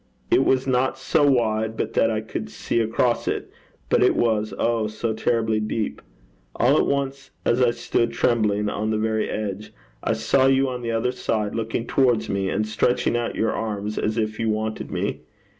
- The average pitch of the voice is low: Yes, low, 115 Hz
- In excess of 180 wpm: Yes, average, 190 wpm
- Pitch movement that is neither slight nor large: No, narrow, 2.3 semitones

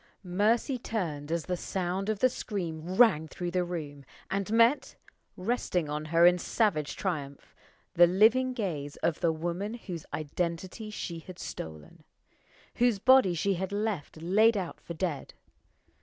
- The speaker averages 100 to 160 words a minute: Yes, average, 150 wpm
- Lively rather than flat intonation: No, average, 4.5 semitones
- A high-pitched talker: No, medium, 180 Hz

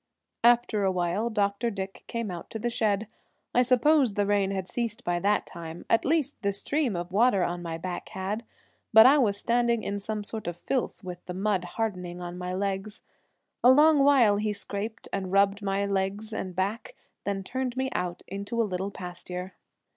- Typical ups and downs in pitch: Yes, average, 3.8 semitones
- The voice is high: Yes, high, 200 Hz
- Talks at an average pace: Yes, average, 190 wpm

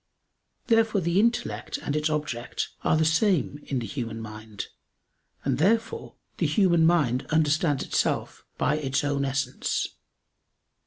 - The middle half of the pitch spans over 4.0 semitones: Yes, average, 4.7 semitones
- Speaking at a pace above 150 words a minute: No, slow, 135 wpm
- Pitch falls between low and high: Yes, medium, 150 Hz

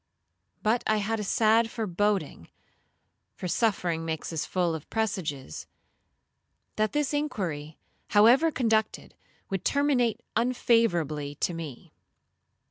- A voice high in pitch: Yes, high, 210 Hz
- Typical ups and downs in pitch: No, wide, 5.8 semitones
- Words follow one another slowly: Yes, slow, 110 wpm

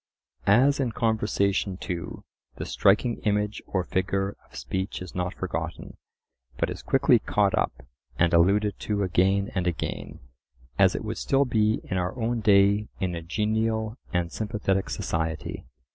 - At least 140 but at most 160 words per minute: Yes, average, 150 wpm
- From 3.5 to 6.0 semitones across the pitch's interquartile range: No, average, 3.1 semitones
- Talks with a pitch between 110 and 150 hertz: No, low, 100 Hz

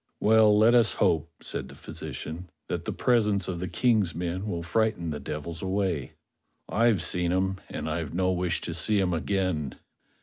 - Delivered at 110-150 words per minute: No, average, 175 wpm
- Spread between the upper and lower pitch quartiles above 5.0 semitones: No, average, 3.7 semitones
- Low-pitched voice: Yes, very low, 90 Hz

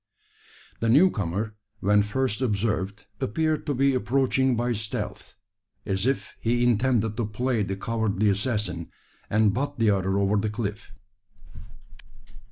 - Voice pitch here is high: No, low, 110 Hz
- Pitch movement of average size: Yes, average, 3.6 semitones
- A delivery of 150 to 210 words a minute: No, slow, 135 wpm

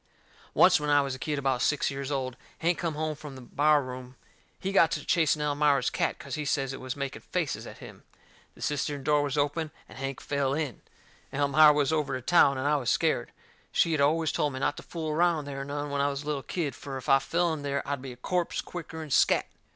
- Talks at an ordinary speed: No, fast, 240 wpm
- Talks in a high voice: No, medium, 145 Hz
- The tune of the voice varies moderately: No, narrow, 2.0 semitones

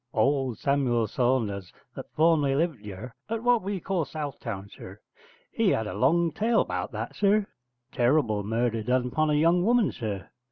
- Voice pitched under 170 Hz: Yes, low, 135 Hz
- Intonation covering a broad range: Yes, wide, 6.9 semitones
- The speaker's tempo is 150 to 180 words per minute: Yes, average, 170 wpm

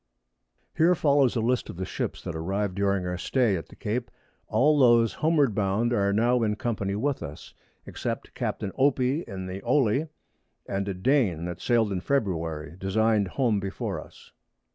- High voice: No, low, 105 Hz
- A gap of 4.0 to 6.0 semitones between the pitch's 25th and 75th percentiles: Yes, average, 4.8 semitones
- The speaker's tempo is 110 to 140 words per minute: No, average, 170 wpm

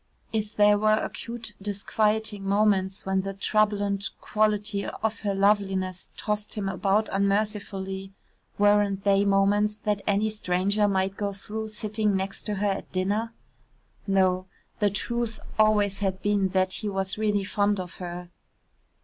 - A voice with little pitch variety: Yes, narrow, 1.5 semitones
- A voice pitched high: Yes, high, 205 Hz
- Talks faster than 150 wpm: No, average, 140 wpm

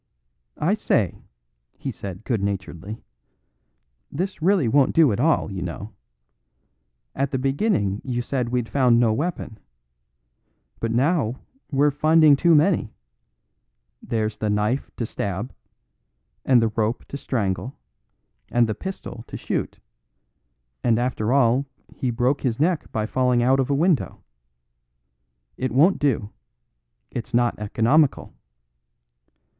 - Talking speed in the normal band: No, slow, 130 wpm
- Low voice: Yes, low, 125 Hz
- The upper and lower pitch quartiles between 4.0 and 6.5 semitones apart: Yes, average, 4.3 semitones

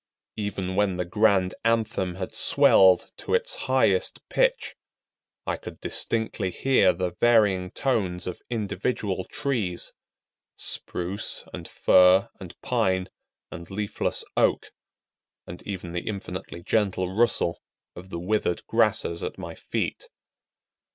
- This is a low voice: Yes, very low, 95 Hz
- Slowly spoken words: Yes, slow, 115 wpm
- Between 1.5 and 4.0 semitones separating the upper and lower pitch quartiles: Yes, average, 3.4 semitones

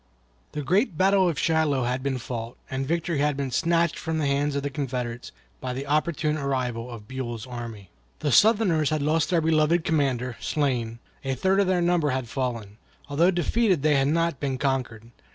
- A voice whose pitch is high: No, medium, 140 Hz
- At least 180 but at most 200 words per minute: Yes, average, 190 wpm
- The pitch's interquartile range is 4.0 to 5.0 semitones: Yes, average, 4.4 semitones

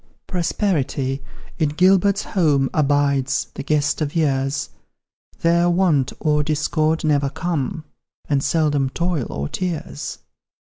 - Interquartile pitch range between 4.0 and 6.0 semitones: No, average, 3.6 semitones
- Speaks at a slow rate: Yes, slow, 110 wpm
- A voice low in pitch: No, medium, 150 Hz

